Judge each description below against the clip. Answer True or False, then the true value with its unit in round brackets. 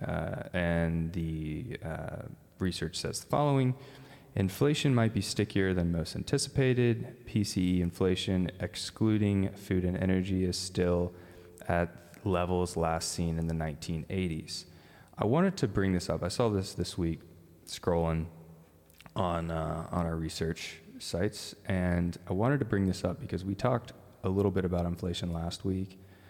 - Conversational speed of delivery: True (150 wpm)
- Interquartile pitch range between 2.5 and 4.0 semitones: True (3.1 semitones)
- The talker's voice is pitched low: True (90 Hz)